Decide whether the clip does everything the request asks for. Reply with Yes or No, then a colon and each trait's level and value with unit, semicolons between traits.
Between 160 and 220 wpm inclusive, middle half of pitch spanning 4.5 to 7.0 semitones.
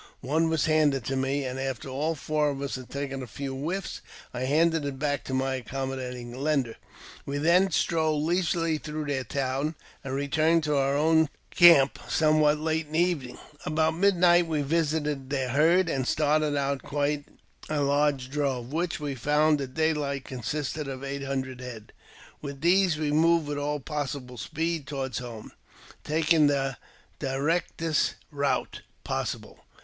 No: average, 165 wpm; average, 2.7 semitones